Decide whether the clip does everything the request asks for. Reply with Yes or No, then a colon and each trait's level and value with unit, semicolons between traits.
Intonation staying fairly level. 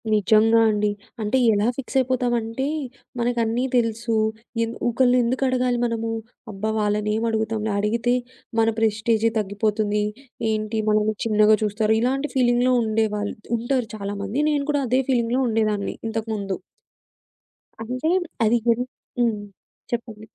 Yes: narrow, 2.2 semitones